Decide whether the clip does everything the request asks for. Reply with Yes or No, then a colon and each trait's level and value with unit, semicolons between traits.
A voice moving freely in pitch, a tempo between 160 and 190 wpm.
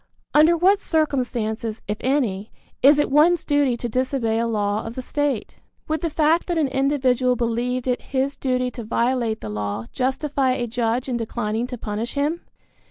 No: average, 4.0 semitones; average, 175 wpm